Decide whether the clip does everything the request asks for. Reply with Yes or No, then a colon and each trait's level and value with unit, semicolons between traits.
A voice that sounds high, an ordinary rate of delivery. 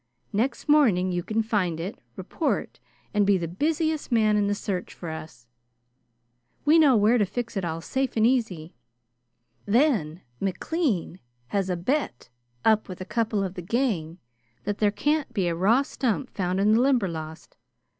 Yes: high, 205 Hz; average, 165 wpm